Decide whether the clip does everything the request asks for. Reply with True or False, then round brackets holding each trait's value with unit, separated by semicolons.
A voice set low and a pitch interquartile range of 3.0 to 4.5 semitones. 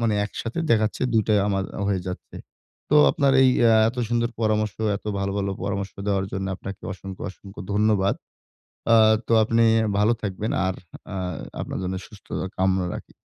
False (105 Hz; 2.5 semitones)